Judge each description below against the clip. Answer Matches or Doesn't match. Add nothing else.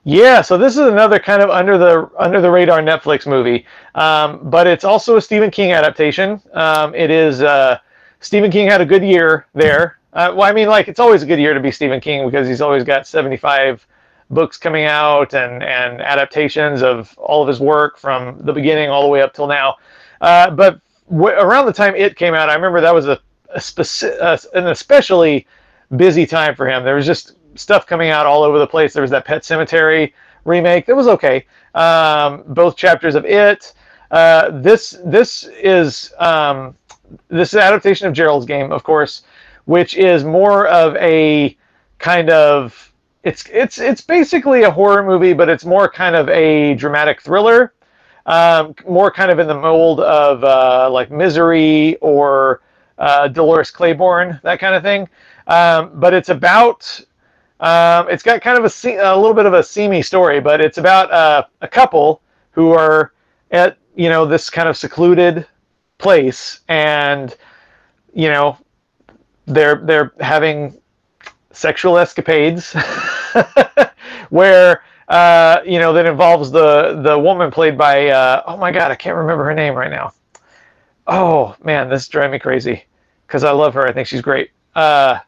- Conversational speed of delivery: Matches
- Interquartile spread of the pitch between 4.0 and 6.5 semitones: Doesn't match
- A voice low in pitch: Doesn't match